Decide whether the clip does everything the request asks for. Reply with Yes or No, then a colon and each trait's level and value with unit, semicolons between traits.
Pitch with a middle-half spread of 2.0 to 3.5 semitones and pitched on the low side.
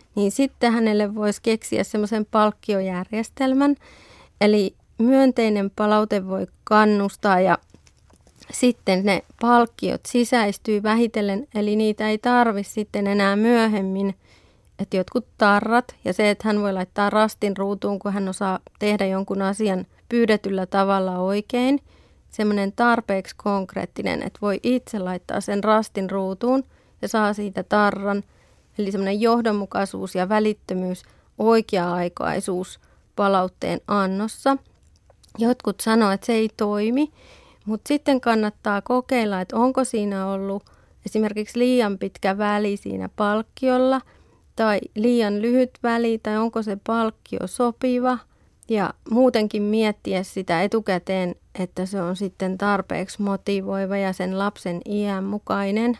No: narrow, 2.6 semitones; high, 210 Hz